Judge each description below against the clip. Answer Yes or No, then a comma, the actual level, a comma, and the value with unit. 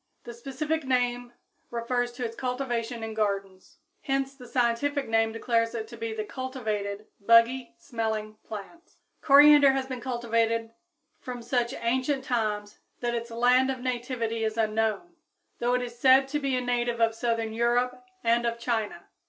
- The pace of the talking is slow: No, average, 160 wpm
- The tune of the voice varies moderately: No, narrow, 2.3 semitones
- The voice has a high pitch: Yes, high, 240 Hz